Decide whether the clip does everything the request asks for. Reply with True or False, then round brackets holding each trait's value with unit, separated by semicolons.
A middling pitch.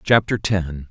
False (95 Hz)